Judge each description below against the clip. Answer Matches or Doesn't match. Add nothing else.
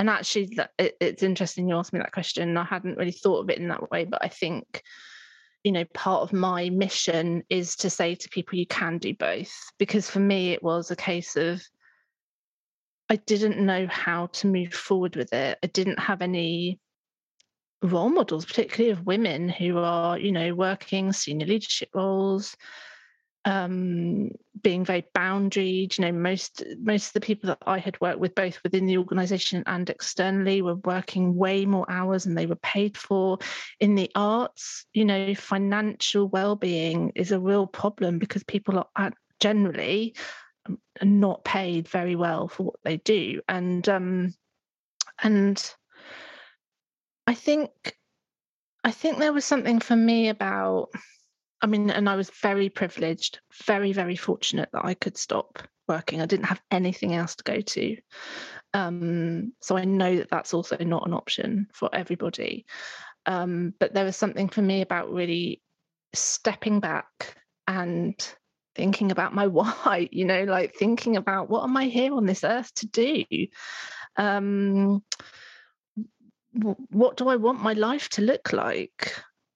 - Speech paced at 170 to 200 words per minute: Doesn't match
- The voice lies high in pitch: Matches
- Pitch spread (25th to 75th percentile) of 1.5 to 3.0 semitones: Matches